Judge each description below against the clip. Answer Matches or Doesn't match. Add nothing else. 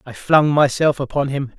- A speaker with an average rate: Matches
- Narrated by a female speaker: Doesn't match